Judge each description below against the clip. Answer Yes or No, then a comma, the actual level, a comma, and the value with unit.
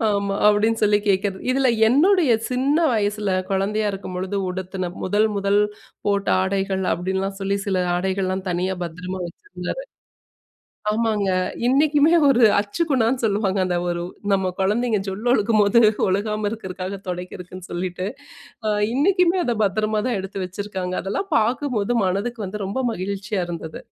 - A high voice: Yes, high, 200 Hz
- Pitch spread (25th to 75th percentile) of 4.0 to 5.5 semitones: No, average, 3.0 semitones